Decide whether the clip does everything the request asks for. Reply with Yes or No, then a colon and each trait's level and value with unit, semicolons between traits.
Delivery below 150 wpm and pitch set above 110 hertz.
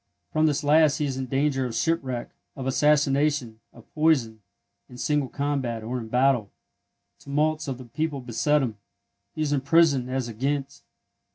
No: average, 165 wpm; low, 135 Hz